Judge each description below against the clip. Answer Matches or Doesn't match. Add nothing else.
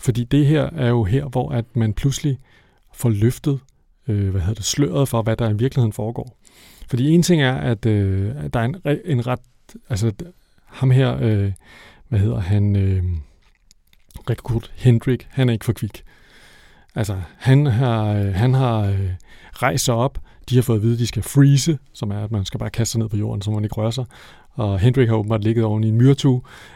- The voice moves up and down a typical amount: Matches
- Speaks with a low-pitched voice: Matches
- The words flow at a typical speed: Matches